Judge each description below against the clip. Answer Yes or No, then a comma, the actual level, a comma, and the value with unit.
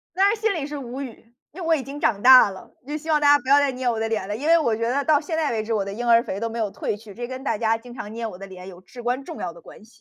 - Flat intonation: No, average, 4.6 semitones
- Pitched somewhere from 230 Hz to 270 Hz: Yes, high, 245 Hz